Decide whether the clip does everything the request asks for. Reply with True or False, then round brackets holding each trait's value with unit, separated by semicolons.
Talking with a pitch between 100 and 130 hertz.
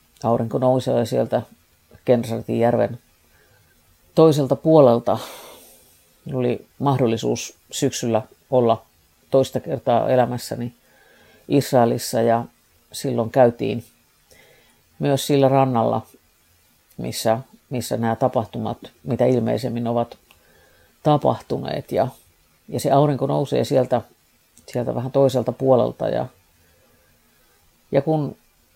True (120 Hz)